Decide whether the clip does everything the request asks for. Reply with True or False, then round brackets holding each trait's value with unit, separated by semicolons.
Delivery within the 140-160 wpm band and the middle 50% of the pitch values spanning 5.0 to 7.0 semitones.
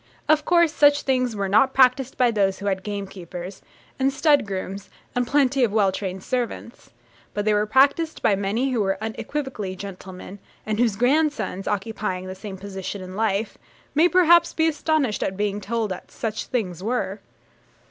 False (170 wpm; 5.4 semitones)